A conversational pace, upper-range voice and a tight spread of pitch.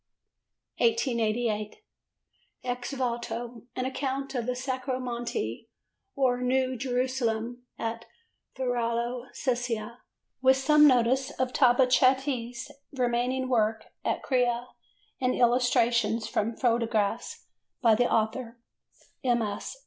No: slow, 95 wpm; high, 245 Hz; narrow, 1.9 semitones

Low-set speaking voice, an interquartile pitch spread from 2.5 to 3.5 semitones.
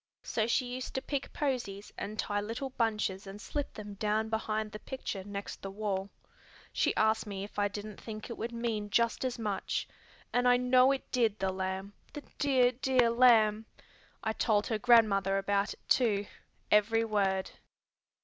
No: high, 215 Hz; average, 3.1 semitones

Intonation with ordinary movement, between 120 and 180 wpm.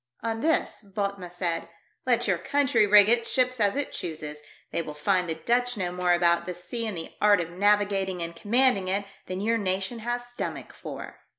No: average, 4.5 semitones; average, 200 wpm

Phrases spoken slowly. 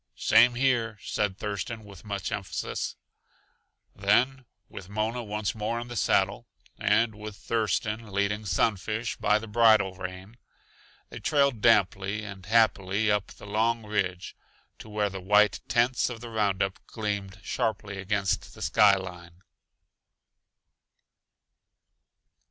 Yes: slow, 125 wpm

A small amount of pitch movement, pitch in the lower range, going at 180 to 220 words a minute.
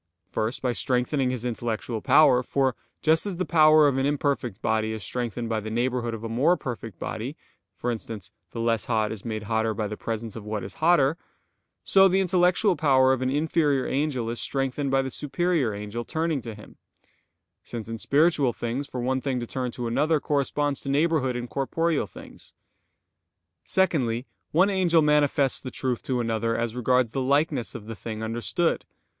No: average, 4.4 semitones; low, 130 Hz; average, 185 wpm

